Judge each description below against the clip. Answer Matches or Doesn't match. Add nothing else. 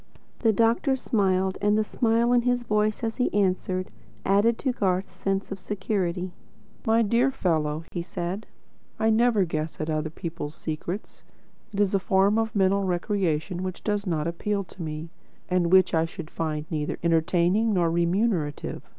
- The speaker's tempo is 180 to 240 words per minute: Doesn't match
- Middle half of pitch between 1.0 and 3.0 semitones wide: Doesn't match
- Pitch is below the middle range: Doesn't match